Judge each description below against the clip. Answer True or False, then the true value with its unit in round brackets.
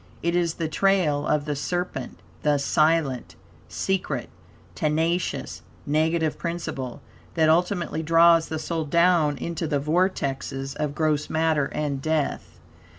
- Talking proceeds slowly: True (125 wpm)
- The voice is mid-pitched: True (160 Hz)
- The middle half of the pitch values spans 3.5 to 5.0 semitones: False (2.4 semitones)